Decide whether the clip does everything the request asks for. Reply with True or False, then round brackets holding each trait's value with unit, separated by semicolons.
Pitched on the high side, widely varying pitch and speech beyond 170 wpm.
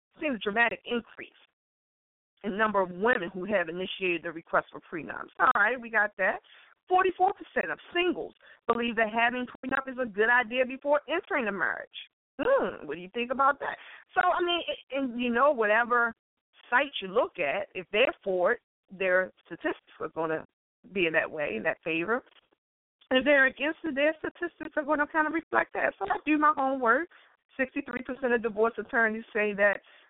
True (250 Hz; 6.2 semitones; 190 wpm)